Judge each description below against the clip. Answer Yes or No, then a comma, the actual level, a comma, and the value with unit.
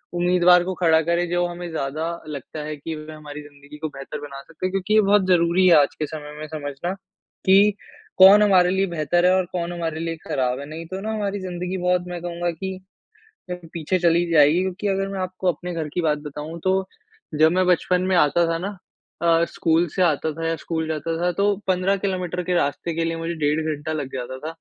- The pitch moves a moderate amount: Yes, average, 3.0 semitones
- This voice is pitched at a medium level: Yes, medium, 170 Hz